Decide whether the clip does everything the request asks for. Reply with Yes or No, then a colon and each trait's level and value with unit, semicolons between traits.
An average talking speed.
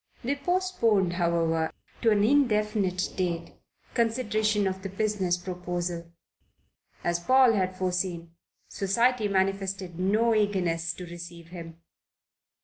No: slow, 110 wpm